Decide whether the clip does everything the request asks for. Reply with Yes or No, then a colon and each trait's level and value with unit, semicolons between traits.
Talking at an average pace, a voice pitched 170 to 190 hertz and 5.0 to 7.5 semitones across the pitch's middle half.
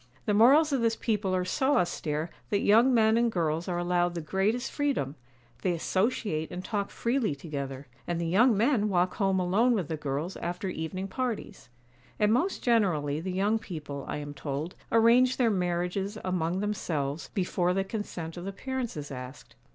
Yes: average, 180 wpm; medium, 185 Hz; wide, 5.4 semitones